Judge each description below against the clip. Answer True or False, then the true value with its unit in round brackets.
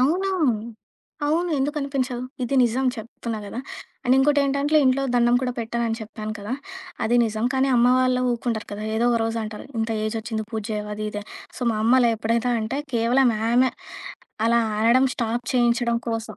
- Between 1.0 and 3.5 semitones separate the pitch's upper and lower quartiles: True (2.5 semitones)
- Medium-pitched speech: False (235 Hz)